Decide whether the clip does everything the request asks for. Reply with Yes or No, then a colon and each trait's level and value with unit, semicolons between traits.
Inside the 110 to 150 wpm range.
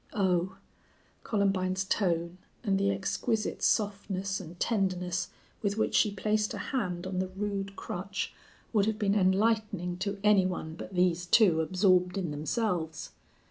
Yes: average, 140 wpm